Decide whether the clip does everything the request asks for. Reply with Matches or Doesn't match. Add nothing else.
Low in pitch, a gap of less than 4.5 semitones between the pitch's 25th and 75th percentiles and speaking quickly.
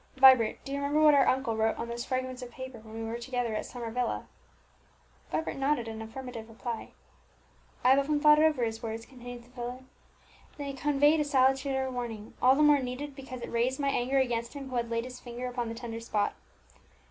Doesn't match